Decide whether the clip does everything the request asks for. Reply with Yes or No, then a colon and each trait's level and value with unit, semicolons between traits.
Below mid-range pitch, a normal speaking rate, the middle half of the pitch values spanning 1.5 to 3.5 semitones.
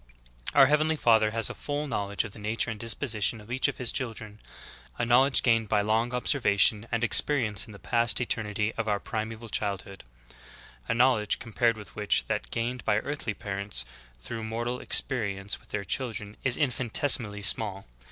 Yes: low, 115 Hz; average, 180 wpm; average, 2.9 semitones